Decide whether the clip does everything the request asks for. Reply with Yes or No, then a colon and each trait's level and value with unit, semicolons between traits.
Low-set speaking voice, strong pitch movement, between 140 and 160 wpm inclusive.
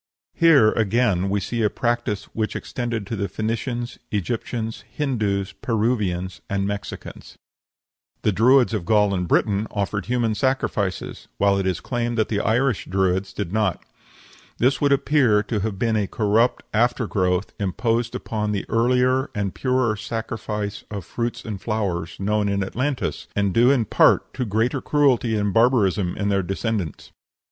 No: low, 110 Hz; average, 3.3 semitones; average, 155 wpm